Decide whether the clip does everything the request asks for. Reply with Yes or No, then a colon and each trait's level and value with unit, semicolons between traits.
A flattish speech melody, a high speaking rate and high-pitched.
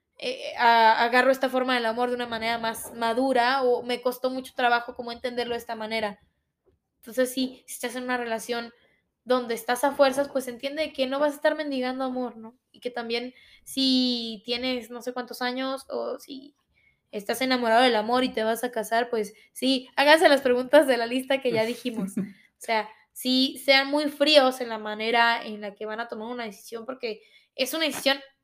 Yes: narrow, 2.3 semitones; fast, 200 wpm; very high, 250 Hz